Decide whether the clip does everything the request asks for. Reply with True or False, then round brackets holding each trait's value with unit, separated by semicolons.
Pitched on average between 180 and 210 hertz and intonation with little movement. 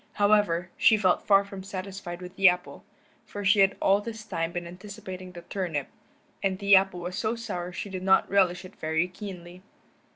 True (190 Hz; 2.1 semitones)